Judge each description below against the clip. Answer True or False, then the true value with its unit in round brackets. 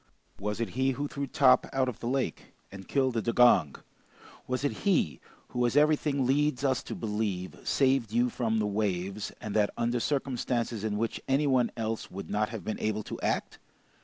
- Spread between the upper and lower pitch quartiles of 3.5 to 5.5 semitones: True (4.0 semitones)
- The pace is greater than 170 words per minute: True (190 wpm)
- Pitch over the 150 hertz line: False (120 Hz)